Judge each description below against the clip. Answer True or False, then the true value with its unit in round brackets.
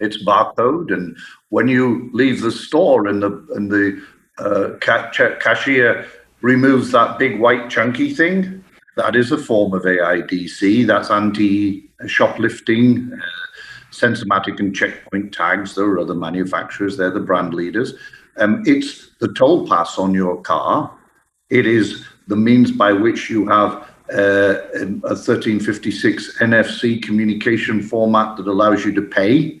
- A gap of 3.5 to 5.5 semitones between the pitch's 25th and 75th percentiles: True (4.0 semitones)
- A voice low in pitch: True (105 Hz)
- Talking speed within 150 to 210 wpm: False (140 wpm)